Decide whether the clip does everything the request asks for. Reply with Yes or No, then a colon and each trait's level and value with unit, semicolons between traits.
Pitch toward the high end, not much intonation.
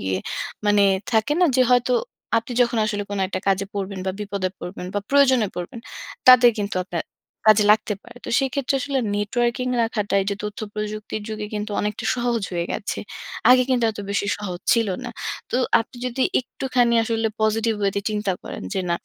No: high, 215 Hz; average, 3.1 semitones